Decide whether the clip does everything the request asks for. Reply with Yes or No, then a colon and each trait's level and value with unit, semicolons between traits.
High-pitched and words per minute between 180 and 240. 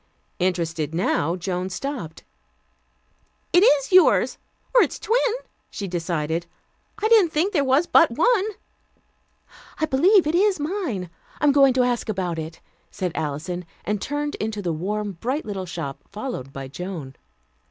No: high, 210 Hz; average, 150 wpm